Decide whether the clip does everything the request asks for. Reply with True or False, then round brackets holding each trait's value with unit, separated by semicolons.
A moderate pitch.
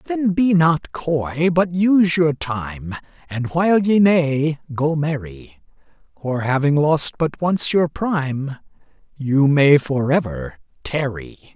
True (155 Hz)